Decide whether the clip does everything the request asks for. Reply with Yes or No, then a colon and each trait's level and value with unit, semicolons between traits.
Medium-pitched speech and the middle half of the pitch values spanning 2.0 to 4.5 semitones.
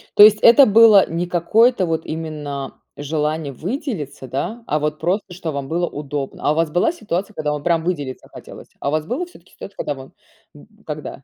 No: medium, 160 Hz; average, 5.0 semitones